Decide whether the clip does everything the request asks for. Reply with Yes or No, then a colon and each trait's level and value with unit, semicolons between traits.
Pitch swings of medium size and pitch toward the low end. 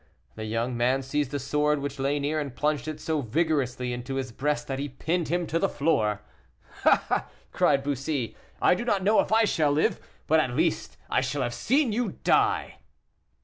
No: average, 3.4 semitones; medium, 145 Hz